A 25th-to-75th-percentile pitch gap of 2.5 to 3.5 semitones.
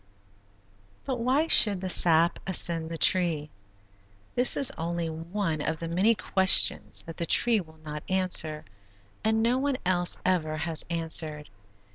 No: average, 4.1 semitones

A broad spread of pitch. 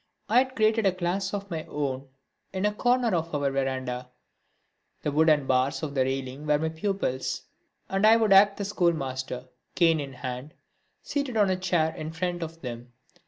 Yes: wide, 6.5 semitones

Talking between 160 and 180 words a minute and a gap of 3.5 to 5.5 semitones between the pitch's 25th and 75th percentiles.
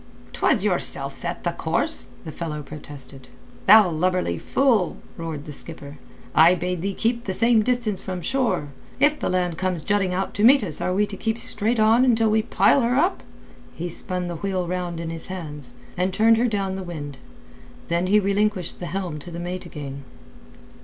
No: average, 190 wpm; average, 4.6 semitones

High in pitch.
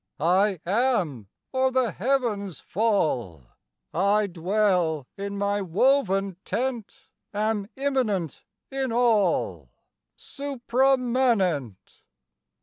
Yes: high, 205 Hz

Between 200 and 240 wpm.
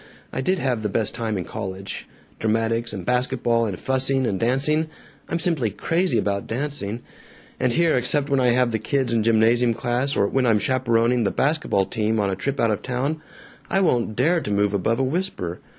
Yes: fast, 205 wpm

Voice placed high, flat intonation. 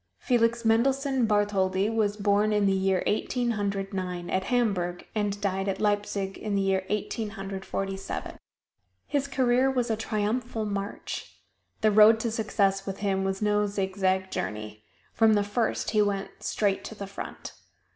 Yes: high, 205 Hz; narrow, 2.3 semitones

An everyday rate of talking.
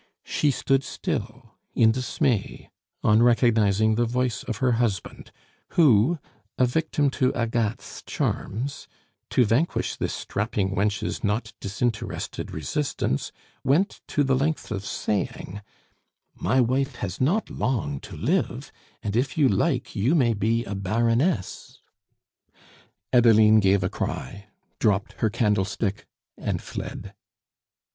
No: slow, 120 wpm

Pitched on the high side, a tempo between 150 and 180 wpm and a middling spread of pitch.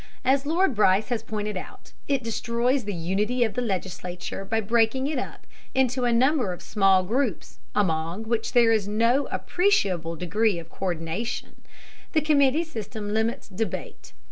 Yes: high, 220 Hz; average, 155 wpm; average, 4.7 semitones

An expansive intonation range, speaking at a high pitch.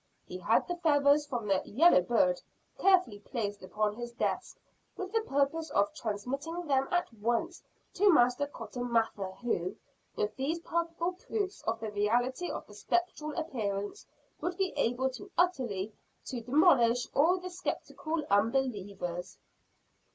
Yes: wide, 7.9 semitones; very high, 255 Hz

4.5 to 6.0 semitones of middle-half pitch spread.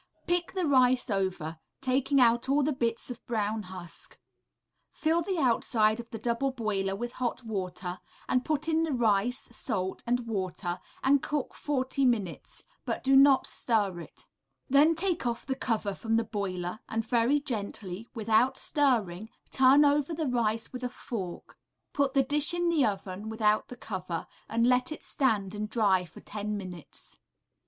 Yes: average, 4.8 semitones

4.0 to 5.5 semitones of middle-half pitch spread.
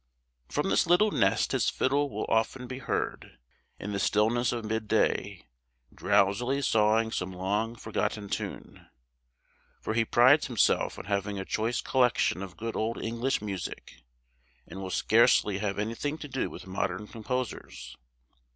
No: average, 3.4 semitones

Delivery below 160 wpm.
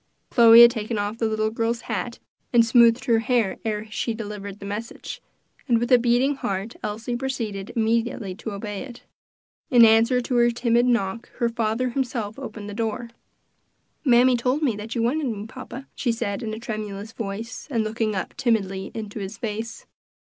No: average, 180 wpm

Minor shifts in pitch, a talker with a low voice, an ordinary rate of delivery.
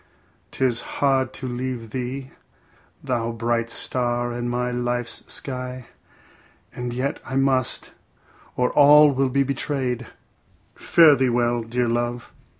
No: narrow, 1.7 semitones; low, 125 Hz; slow, 125 wpm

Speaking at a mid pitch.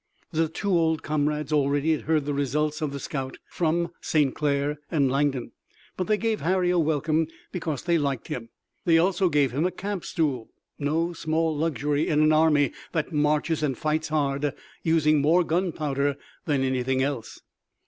Yes: medium, 150 Hz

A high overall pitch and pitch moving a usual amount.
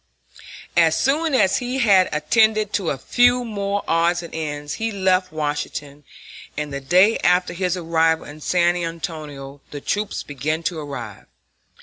No: medium, 170 Hz; average, 5.0 semitones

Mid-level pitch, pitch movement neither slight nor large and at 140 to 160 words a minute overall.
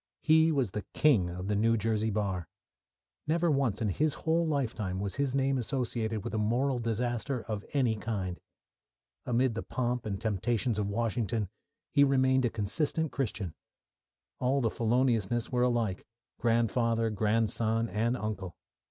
No: low, 115 Hz; average, 3.5 semitones; average, 150 wpm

